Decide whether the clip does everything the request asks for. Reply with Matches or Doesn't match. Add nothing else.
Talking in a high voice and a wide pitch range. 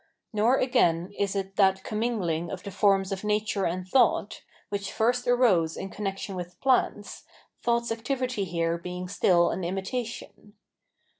Doesn't match